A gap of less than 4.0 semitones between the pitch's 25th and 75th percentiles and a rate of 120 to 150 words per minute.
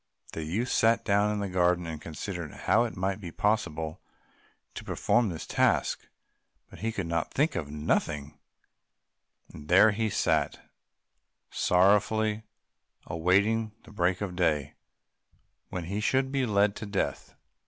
No: average, 4.4 semitones; average, 140 wpm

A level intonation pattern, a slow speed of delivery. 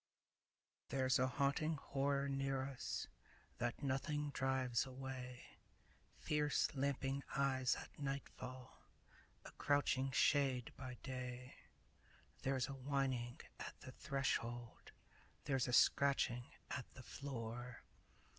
Yes: narrow, 1.6 semitones; slow, 105 wpm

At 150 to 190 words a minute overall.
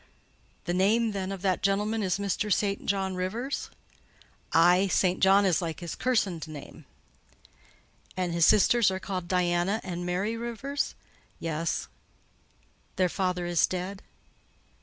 No: slow, 135 wpm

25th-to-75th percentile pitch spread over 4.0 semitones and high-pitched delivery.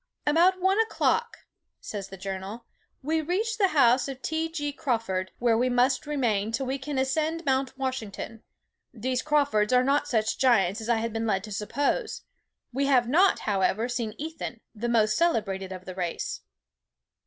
Yes: wide, 5.4 semitones; very high, 250 Hz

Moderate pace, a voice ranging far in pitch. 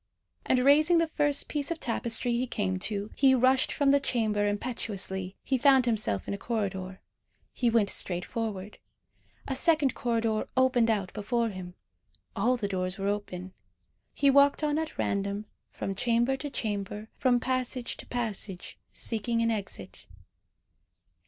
No: average, 150 wpm; average, 4.5 semitones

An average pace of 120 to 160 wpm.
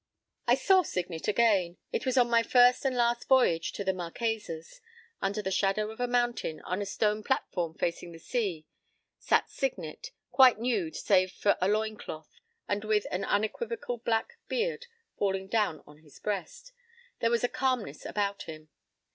No: average, 170 wpm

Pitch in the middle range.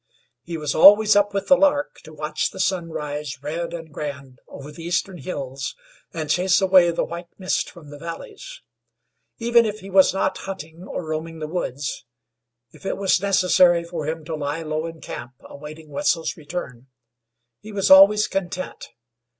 Yes: medium, 170 Hz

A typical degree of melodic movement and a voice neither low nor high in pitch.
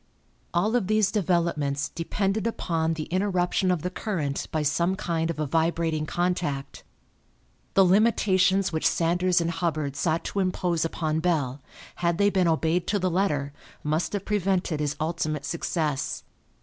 Yes: average, 3.1 semitones; medium, 170 Hz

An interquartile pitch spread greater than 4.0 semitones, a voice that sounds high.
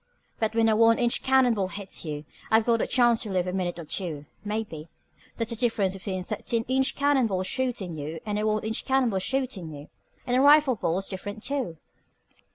Yes: average, 4.7 semitones; high, 215 Hz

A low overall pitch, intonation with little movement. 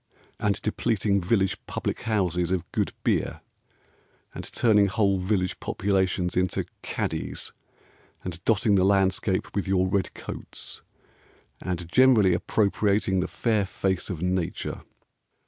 Yes: very low, 95 Hz; narrow, 2.0 semitones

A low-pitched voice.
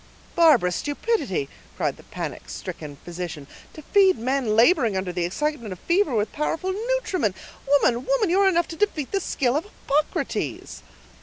No: very high, 285 Hz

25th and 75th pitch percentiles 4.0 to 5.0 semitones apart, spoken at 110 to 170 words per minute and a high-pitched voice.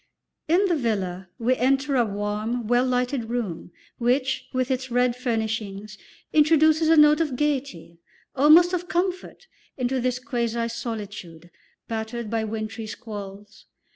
Yes: average, 4.4 semitones; slow, 135 wpm; high, 245 Hz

